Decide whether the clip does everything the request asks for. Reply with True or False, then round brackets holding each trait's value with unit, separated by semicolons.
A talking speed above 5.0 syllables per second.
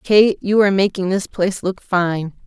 False (4.9 syllables/s)